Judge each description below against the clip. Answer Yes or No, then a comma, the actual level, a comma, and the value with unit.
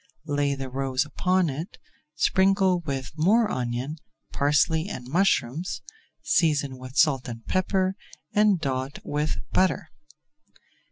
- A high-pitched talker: No, medium, 150 Hz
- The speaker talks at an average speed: No, slow, 115 wpm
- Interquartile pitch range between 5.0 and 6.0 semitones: Yes, wide, 5.5 semitones